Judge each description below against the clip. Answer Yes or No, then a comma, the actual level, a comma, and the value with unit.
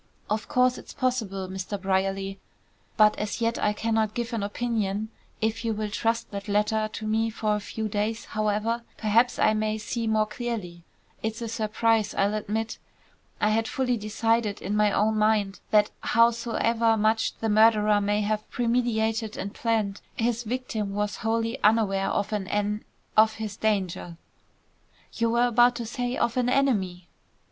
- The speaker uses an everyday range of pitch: No, narrow, 1.7 semitones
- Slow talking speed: No, average, 165 wpm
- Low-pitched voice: No, high, 220 Hz